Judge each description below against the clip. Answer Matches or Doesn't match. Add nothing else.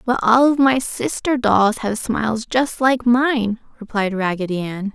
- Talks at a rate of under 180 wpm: Matches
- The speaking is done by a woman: Matches